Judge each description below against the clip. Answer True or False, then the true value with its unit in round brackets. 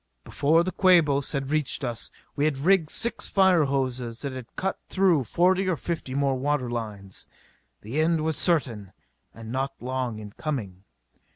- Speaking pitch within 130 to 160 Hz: True (140 Hz)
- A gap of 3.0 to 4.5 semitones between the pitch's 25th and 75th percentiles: False (5.2 semitones)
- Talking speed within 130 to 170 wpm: True (165 wpm)